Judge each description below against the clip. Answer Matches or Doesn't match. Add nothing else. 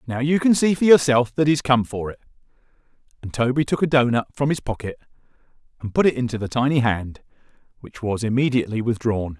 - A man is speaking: Matches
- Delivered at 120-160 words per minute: Doesn't match